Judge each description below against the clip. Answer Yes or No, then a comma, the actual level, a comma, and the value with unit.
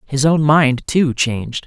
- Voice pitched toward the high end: No, medium, 140 Hz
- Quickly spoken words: No, average, 180 wpm